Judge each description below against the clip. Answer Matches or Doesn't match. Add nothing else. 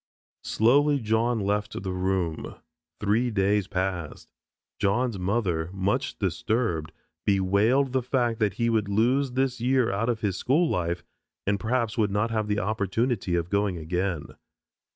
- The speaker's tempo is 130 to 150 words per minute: Matches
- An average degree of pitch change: Matches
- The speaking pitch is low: Matches